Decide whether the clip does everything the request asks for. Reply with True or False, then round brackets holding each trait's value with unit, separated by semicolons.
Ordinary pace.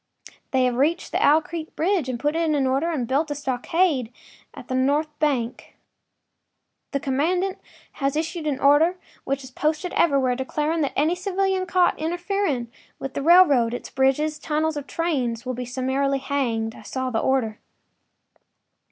True (160 wpm)